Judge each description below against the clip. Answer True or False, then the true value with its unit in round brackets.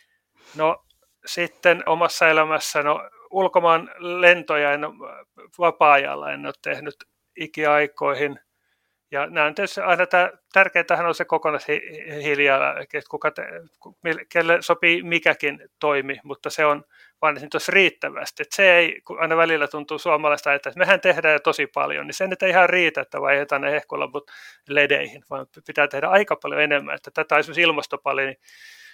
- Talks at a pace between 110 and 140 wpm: False (150 wpm)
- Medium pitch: True (160 Hz)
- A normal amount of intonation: True (3.1 semitones)